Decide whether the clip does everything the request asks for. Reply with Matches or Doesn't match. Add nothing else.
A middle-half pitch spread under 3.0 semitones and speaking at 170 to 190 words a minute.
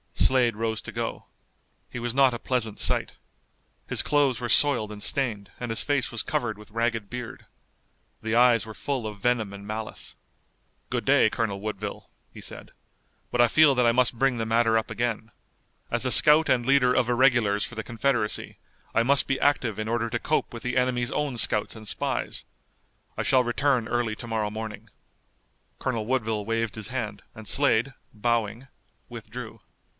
Matches